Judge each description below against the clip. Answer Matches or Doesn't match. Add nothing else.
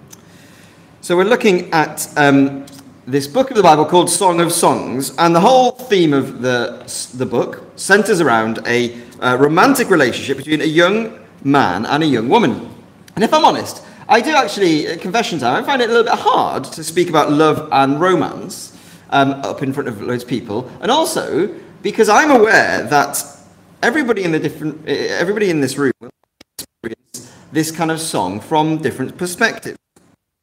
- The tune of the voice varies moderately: Doesn't match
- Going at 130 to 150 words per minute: Doesn't match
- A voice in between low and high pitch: Matches